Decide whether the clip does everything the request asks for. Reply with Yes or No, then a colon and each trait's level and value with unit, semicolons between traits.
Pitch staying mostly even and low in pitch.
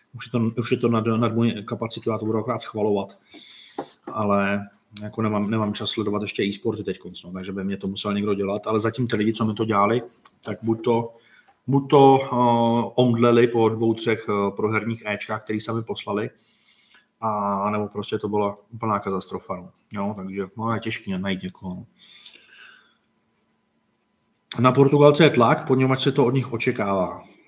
Yes: narrow, 2.3 semitones; low, 110 Hz